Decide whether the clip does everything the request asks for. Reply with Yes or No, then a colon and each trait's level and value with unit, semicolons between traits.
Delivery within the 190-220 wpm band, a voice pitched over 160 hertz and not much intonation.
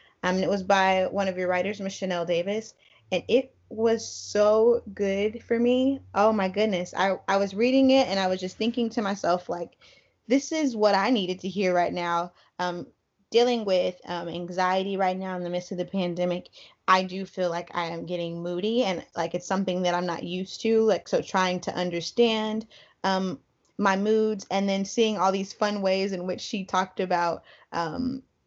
No: average, 200 wpm; high, 190 Hz; average, 3.2 semitones